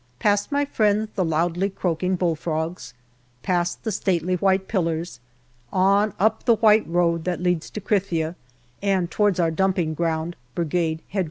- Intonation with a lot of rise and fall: No, average, 3.1 semitones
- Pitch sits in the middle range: Yes, medium, 180 Hz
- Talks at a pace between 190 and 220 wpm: No, average, 155 wpm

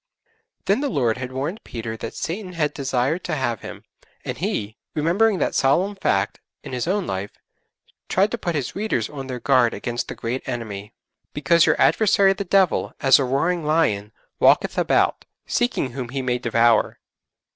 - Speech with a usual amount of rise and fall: No, wide, 7.0 semitones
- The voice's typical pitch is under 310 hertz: Yes, low, 135 Hz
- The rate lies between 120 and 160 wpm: No, average, 175 wpm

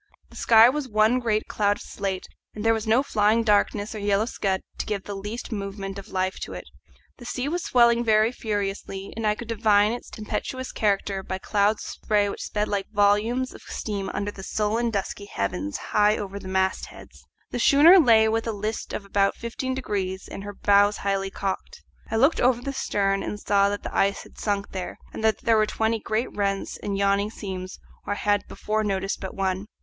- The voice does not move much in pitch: Yes, narrow, 2.1 semitones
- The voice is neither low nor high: No, high, 210 Hz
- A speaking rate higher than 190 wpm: Yes, fast, 205 wpm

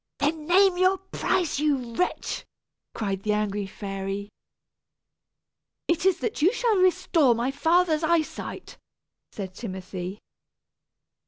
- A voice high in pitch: Yes, very high, 295 Hz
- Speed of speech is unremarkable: No, slow, 115 wpm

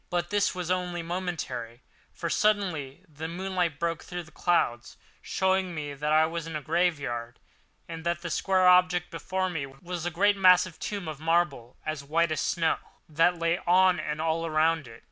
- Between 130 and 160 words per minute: No, average, 185 wpm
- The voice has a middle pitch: Yes, medium, 170 Hz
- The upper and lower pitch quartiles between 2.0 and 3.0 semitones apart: Yes, average, 2.7 semitones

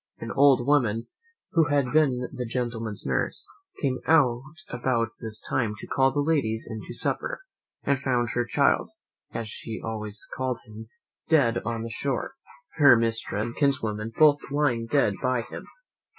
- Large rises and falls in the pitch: No, average, 3.6 semitones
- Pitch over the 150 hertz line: No, low, 120 Hz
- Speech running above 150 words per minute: Yes, average, 160 wpm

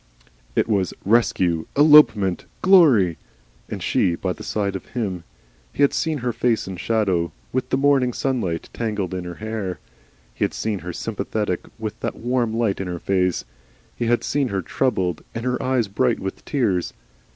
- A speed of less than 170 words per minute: No, average, 175 wpm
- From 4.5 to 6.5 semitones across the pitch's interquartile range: Yes, average, 5.1 semitones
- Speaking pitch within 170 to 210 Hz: No, low, 110 Hz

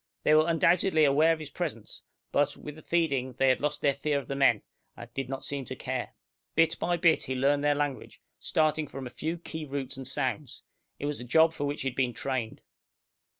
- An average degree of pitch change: Yes, average, 3.0 semitones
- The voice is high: No, medium, 145 Hz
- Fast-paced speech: Yes, fast, 225 wpm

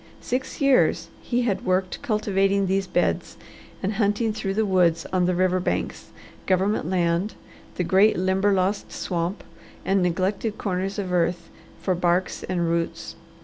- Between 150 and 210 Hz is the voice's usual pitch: Yes, high, 190 Hz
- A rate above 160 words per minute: No, average, 145 wpm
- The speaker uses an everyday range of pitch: No, narrow, 2.2 semitones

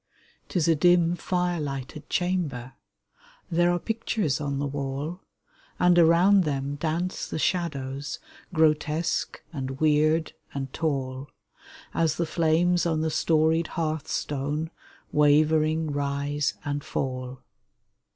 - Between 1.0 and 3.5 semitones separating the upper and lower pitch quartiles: Yes, average, 3.0 semitones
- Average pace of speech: No, slow, 115 wpm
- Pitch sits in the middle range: Yes, medium, 155 Hz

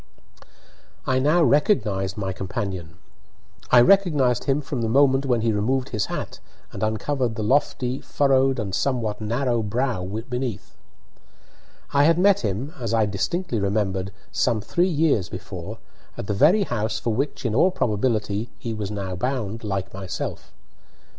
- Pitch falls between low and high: No, low, 115 Hz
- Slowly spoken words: No, average, 150 wpm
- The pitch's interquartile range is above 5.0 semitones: No, average, 4.6 semitones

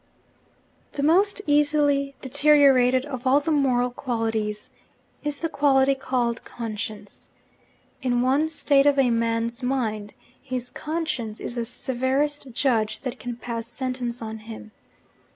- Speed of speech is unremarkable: No, slow, 130 wpm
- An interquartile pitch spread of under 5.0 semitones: Yes, average, 3.4 semitones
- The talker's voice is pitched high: Yes, very high, 255 Hz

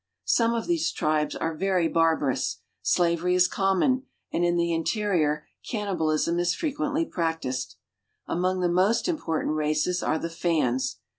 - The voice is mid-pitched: Yes, medium, 170 Hz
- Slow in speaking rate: No, average, 145 wpm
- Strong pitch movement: No, average, 3.5 semitones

